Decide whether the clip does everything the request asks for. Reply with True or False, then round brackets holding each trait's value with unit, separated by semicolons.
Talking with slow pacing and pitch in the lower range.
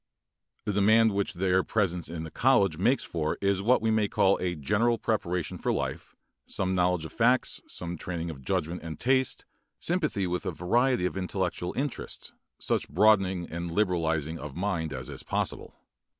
False (170 wpm; 90 Hz)